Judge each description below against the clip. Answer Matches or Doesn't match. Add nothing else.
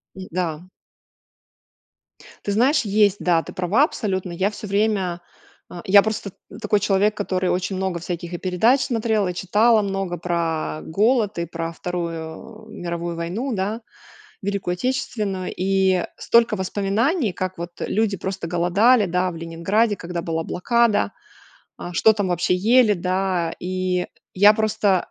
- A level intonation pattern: Doesn't match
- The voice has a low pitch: Doesn't match